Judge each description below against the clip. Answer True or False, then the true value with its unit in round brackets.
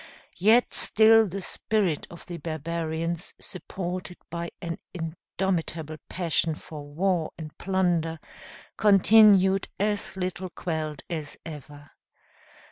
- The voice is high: False (170 Hz)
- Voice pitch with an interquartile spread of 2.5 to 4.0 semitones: True (3.1 semitones)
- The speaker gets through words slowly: True (105 wpm)